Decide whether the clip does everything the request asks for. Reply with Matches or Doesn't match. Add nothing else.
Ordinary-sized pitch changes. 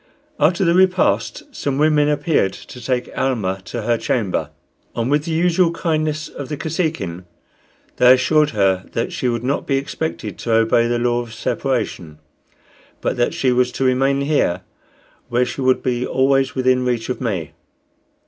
Matches